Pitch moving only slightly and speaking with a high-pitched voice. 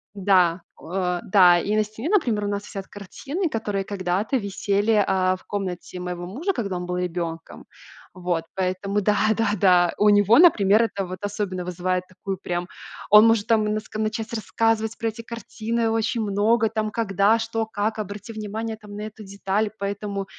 No: average, 3.0 semitones; high, 205 Hz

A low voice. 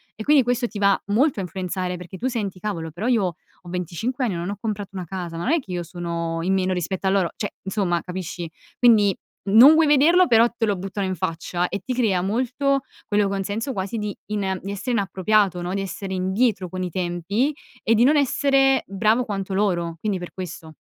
No: high, 195 Hz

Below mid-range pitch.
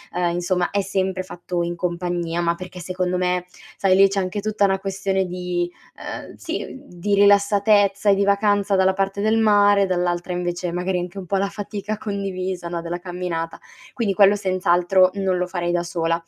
No: medium, 185 Hz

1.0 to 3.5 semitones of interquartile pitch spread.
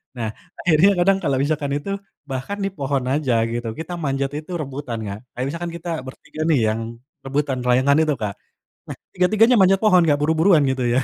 No: average, 4.6 semitones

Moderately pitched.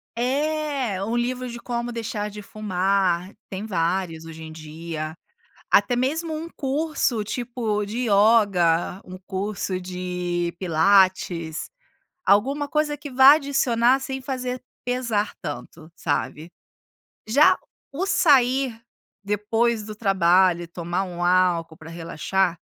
No: high, 205 Hz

